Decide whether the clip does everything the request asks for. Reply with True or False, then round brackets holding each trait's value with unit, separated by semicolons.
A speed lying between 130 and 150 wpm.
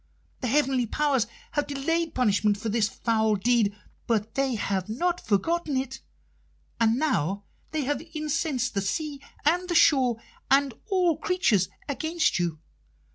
True (140 wpm)